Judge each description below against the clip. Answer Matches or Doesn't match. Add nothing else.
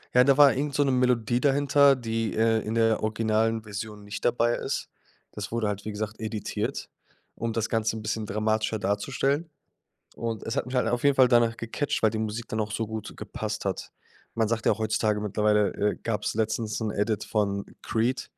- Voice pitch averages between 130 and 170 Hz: Doesn't match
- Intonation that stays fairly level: Matches